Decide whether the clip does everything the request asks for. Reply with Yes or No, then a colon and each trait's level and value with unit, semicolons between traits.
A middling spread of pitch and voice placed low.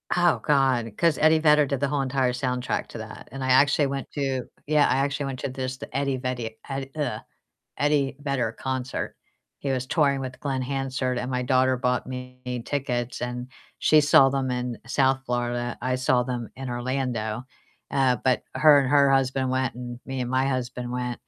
No: narrow, 1.7 semitones; low, 130 Hz